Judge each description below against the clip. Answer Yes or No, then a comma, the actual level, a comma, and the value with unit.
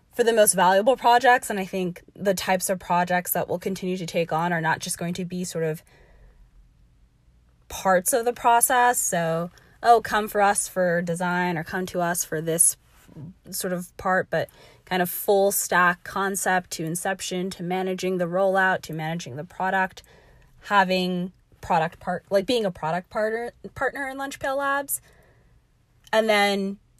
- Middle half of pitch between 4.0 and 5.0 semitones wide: No, average, 2.8 semitones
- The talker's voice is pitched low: No, medium, 185 Hz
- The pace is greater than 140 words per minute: Yes, average, 170 wpm